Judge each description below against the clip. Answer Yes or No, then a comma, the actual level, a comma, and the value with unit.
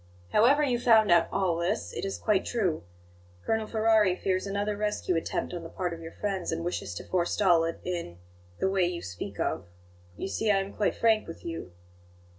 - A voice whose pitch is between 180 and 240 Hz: Yes, high, 190 Hz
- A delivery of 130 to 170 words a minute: No, average, 200 wpm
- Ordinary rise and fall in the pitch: Yes, average, 3.8 semitones